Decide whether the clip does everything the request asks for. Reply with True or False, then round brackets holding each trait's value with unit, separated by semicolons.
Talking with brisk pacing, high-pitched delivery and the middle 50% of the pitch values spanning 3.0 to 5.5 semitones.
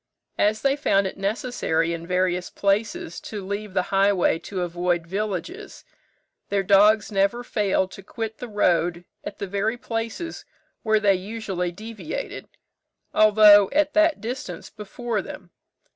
False (140 wpm; 205 Hz; 3.3 semitones)